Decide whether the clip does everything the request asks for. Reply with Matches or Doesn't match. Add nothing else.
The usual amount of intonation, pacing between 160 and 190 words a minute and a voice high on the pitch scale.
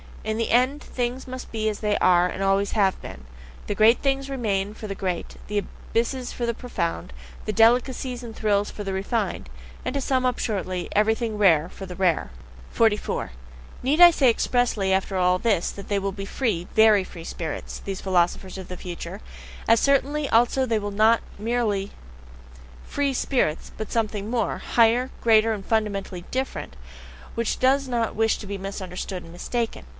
Matches